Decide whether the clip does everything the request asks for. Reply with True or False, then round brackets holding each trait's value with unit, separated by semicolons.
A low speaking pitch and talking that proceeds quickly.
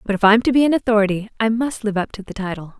False (215 Hz; 300 wpm)